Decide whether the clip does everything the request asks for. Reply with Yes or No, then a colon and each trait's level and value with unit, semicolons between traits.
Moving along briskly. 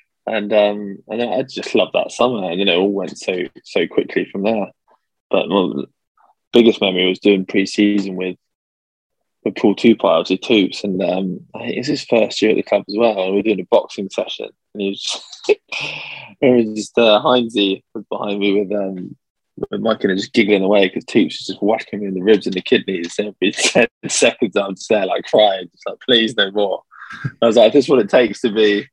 Yes: fast, 235 wpm